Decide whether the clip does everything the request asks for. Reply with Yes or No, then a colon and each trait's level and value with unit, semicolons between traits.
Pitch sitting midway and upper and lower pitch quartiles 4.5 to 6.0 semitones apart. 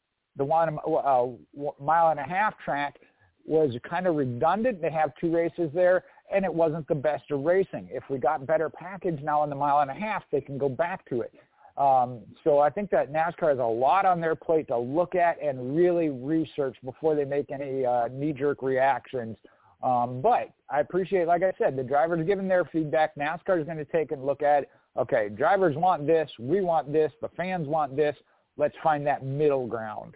No: medium, 155 Hz; average, 3.3 semitones